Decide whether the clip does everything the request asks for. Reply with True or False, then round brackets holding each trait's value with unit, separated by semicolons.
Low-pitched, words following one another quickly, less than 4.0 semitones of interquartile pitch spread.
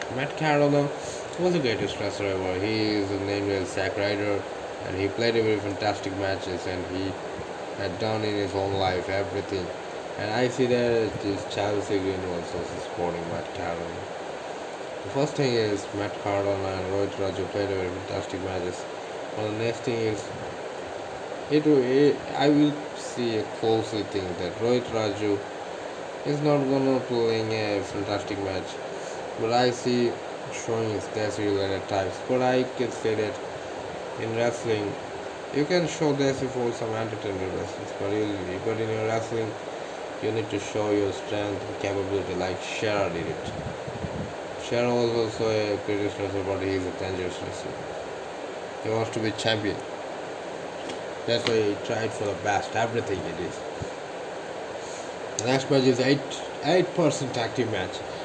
False (105 Hz; 160 wpm; 3.3 semitones)